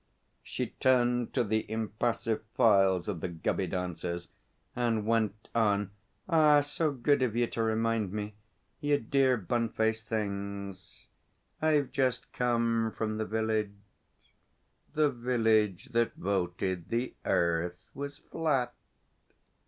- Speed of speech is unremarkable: No, slow, 120 wpm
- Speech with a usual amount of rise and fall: Yes, average, 3.5 semitones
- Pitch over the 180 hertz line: No, low, 110 Hz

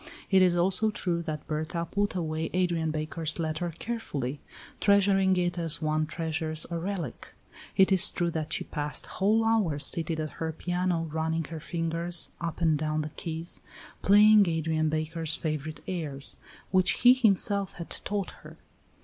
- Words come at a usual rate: Yes, average, 160 wpm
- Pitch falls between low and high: Yes, medium, 165 Hz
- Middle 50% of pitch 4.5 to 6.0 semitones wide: No, average, 3.0 semitones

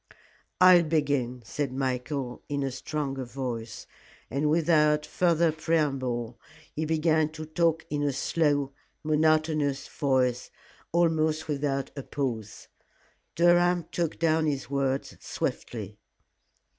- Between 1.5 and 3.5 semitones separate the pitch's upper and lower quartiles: Yes, average, 2.8 semitones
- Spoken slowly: Yes, slow, 110 wpm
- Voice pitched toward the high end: No, medium, 150 Hz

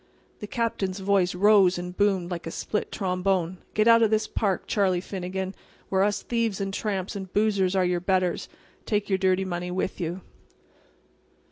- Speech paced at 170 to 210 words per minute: Yes, average, 175 wpm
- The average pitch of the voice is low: No, high, 190 Hz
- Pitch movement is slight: Yes, narrow, 2.1 semitones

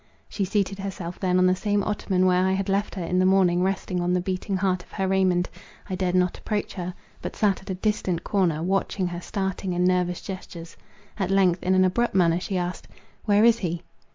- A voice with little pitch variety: Yes, narrow, 1.4 semitones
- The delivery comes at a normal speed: No, fast, 220 wpm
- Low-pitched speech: No, medium, 185 Hz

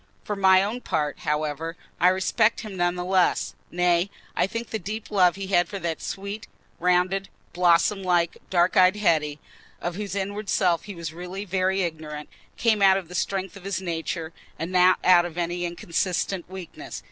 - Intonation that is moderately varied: No, narrow, 2.3 semitones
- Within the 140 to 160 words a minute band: No, average, 180 wpm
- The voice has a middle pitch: Yes, medium, 180 Hz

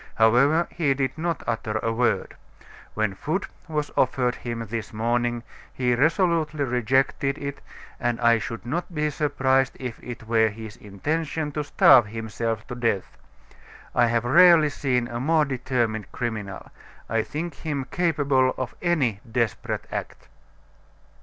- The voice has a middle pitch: No, low, 125 Hz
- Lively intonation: No, average, 4.3 semitones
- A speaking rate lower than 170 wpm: Yes, average, 140 wpm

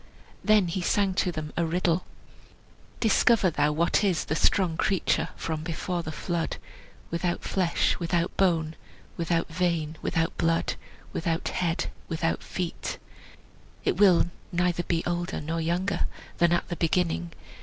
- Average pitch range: No, narrow, 1.8 semitones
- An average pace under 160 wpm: Yes, average, 140 wpm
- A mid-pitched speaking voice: Yes, medium, 170 Hz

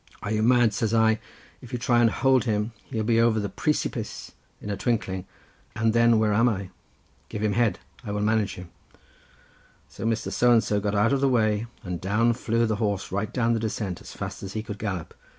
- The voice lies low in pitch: Yes, low, 110 Hz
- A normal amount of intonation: No, narrow, 2.2 semitones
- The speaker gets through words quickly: Yes, fast, 225 wpm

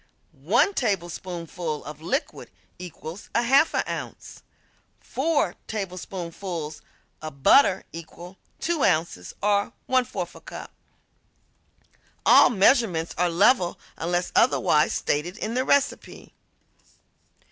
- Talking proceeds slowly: Yes, slow, 95 wpm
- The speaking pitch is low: No, medium, 180 Hz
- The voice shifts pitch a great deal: Yes, wide, 6.1 semitones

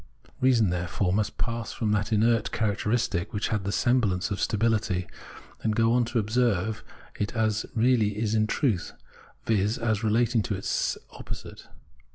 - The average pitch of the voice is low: Yes, low, 110 Hz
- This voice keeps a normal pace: Yes, average, 170 wpm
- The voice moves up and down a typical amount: No, narrow, 2.1 semitones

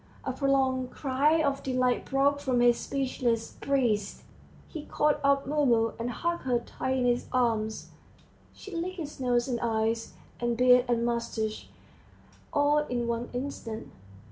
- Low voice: No, very high, 255 Hz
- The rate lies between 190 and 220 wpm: No, average, 145 wpm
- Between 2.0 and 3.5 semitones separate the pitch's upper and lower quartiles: Yes, average, 2.9 semitones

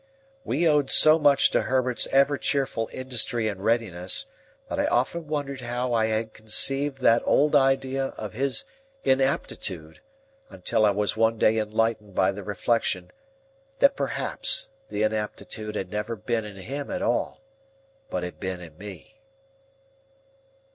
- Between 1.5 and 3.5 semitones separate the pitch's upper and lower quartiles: No, average, 4.5 semitones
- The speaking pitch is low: Yes, low, 115 Hz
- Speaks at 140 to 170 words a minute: Yes, average, 145 wpm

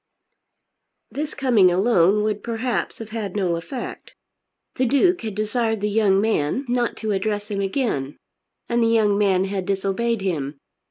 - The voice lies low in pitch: No, high, 210 Hz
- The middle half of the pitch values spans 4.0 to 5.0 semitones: No, average, 3.3 semitones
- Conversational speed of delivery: Yes, average, 155 wpm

